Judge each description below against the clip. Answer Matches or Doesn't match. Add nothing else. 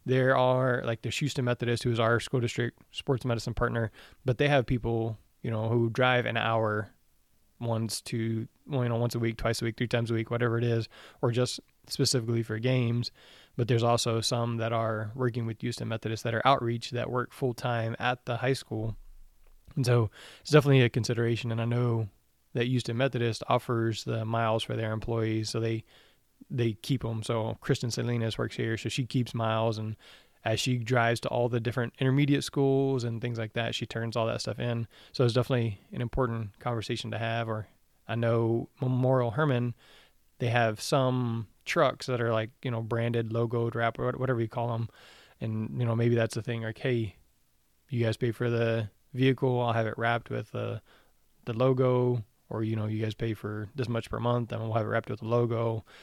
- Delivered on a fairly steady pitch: Matches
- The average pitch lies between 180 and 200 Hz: Doesn't match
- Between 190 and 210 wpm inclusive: Matches